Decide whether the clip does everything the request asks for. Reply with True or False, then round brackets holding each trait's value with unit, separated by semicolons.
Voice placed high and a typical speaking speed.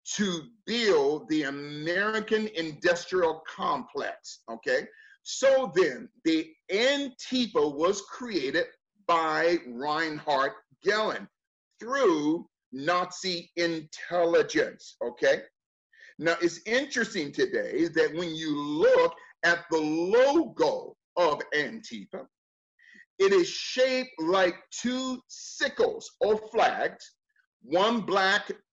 False (230 Hz; 90 wpm)